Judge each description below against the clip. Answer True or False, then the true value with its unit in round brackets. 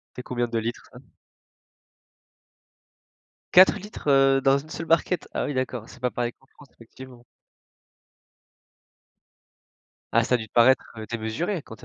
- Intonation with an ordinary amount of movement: True (3.0 semitones)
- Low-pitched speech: True (130 Hz)